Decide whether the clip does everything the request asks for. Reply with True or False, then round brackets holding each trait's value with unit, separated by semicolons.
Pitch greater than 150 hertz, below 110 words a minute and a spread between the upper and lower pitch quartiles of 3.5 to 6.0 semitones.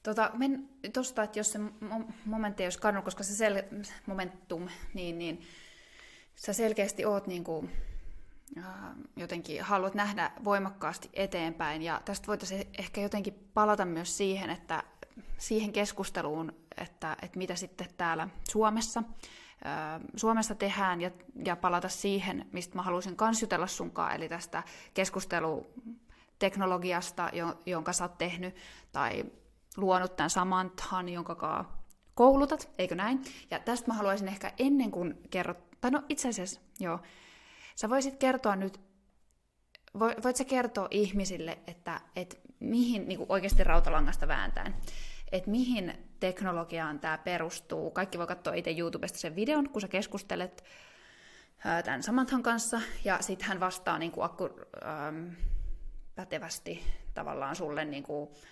False (190 Hz; 130 wpm; 3.8 semitones)